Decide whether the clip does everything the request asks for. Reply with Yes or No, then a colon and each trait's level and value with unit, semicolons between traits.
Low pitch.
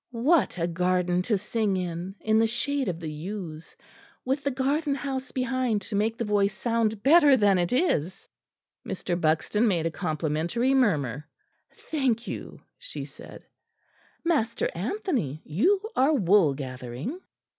No: high, 210 Hz